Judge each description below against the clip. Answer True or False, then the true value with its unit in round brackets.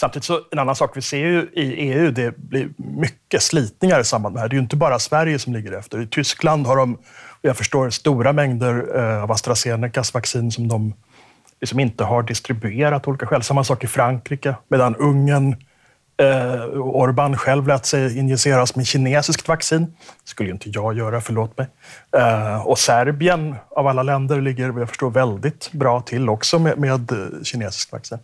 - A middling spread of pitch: True (3.2 semitones)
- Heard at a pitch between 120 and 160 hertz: True (130 Hz)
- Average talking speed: True (185 wpm)